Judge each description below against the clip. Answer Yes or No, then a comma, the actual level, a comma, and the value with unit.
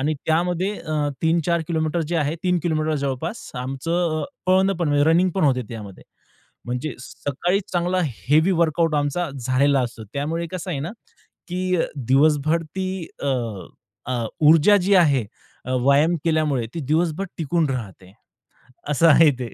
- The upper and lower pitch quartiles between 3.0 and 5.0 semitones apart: Yes, average, 3.6 semitones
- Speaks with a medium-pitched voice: Yes, medium, 155 Hz